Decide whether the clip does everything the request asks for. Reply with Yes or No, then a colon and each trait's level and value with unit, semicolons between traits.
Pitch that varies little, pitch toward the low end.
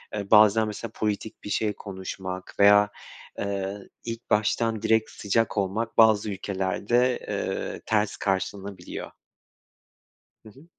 Yes: narrow, 2.0 semitones; low, 105 Hz